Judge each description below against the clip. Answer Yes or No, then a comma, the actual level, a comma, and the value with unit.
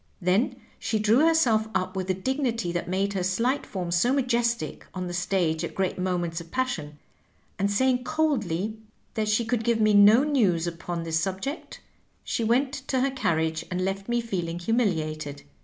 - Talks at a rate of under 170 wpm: No, average, 175 wpm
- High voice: Yes, high, 200 Hz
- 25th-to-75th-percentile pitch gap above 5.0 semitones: Yes, wide, 5.4 semitones